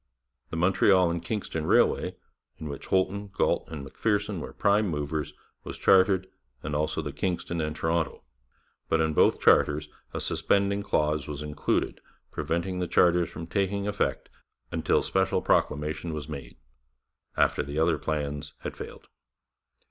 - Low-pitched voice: Yes, very low, 80 Hz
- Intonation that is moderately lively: Yes, average, 3.9 semitones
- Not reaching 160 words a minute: Yes, average, 145 wpm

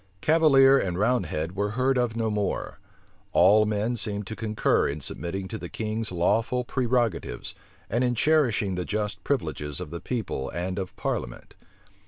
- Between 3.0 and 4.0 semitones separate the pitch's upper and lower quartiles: No, average, 4.7 semitones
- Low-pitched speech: Yes, low, 110 Hz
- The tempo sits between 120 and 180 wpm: Yes, average, 160 wpm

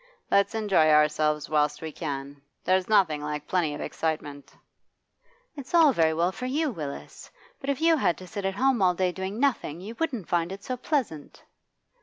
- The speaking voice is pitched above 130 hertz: Yes, medium, 185 Hz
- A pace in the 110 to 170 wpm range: No, average, 185 wpm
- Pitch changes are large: Yes, wide, 7.5 semitones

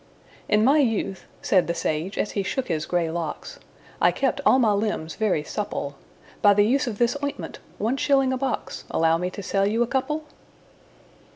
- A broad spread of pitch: Yes, wide, 6.3 semitones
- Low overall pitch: No, high, 210 Hz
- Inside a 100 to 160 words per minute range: No, average, 190 wpm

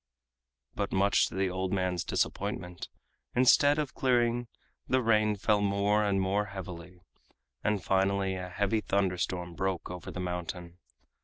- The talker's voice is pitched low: Yes, very low, 95 Hz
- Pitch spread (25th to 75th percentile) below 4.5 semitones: Yes, narrow, 2.5 semitones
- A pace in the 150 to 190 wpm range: No, average, 140 wpm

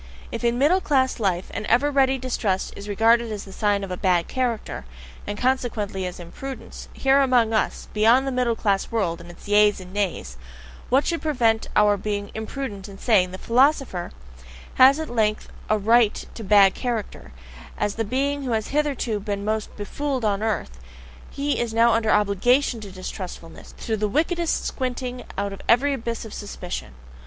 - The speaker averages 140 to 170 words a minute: No, average, 180 wpm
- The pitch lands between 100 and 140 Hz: No, high, 220 Hz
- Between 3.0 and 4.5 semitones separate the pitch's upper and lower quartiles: Yes, average, 4.2 semitones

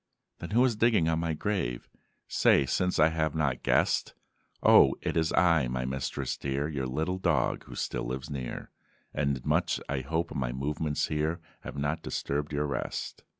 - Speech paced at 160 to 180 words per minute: Yes, average, 175 wpm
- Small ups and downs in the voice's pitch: No, average, 3.4 semitones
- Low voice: Yes, very low, 75 Hz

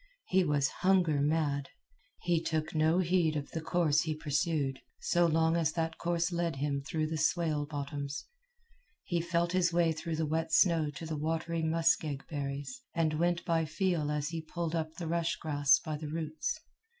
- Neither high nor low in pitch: Yes, medium, 160 Hz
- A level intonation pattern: Yes, narrow, 2.1 semitones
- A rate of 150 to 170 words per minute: No, average, 180 wpm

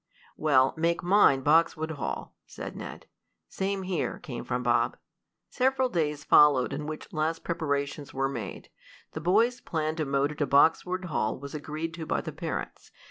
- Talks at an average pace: Yes, average, 165 wpm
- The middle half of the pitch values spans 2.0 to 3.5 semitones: Yes, average, 3.2 semitones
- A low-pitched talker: No, medium, 155 Hz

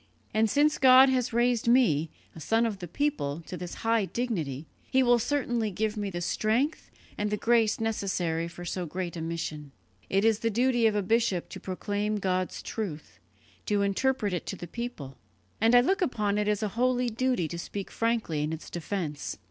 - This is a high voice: Yes, high, 210 Hz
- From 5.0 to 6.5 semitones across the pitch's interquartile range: Yes, average, 5.3 semitones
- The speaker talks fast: No, average, 195 wpm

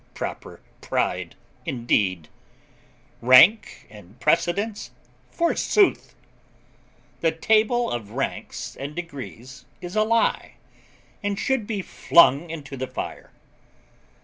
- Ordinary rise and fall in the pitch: No, wide, 9.0 semitones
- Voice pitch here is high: No, medium, 165 Hz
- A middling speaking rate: No, slow, 95 wpm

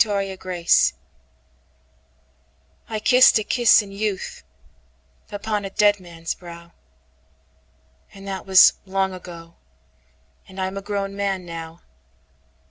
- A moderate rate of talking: No, slow, 95 wpm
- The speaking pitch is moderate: Yes, medium, 180 Hz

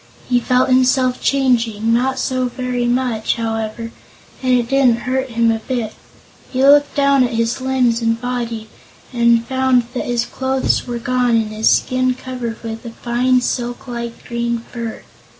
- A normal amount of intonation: No, narrow, 1.9 semitones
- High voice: Yes, high, 245 Hz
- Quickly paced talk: No, average, 165 wpm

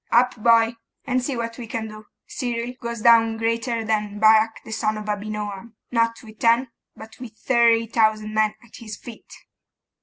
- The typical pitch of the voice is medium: No, high, 225 Hz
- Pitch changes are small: Yes, narrow, 1.5 semitones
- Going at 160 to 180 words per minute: Yes, average, 175 wpm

